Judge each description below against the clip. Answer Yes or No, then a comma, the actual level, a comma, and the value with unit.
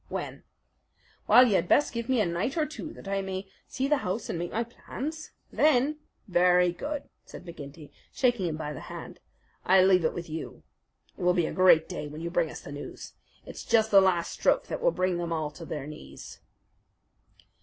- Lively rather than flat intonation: Yes, wide, 6.1 semitones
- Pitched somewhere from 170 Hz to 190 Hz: Yes, medium, 185 Hz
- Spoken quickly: Yes, fast, 210 wpm